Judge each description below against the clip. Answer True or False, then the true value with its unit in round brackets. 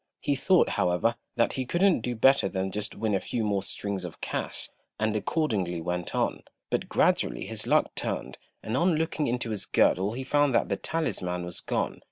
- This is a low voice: True (110 Hz)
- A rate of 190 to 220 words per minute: True (195 wpm)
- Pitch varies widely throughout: True (6.3 semitones)